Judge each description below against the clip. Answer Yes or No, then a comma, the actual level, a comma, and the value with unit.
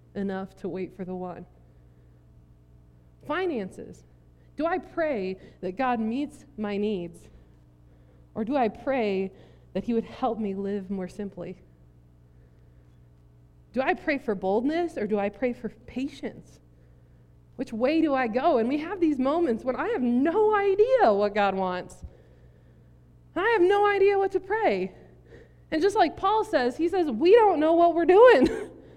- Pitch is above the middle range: Yes, high, 205 Hz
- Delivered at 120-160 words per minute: Yes, average, 155 wpm